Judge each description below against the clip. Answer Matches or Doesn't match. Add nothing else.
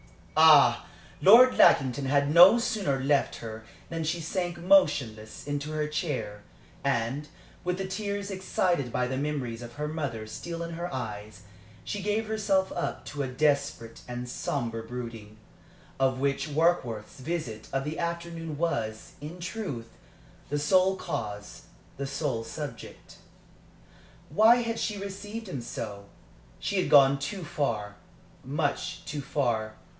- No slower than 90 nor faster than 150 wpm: Matches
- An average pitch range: Doesn't match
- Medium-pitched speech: Matches